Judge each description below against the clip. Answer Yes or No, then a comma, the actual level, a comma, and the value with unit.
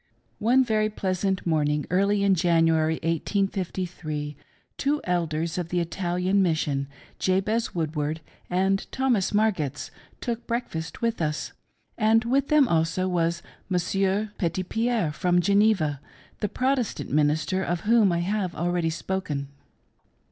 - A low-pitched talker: No, medium, 180 Hz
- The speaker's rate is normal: No, slow, 120 wpm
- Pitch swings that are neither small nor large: Yes, average, 4.3 semitones